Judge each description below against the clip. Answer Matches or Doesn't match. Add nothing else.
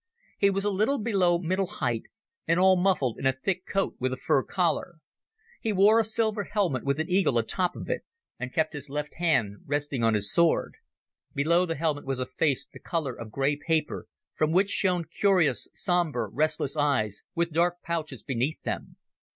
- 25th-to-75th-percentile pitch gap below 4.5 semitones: Doesn't match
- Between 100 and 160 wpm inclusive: Doesn't match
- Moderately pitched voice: Matches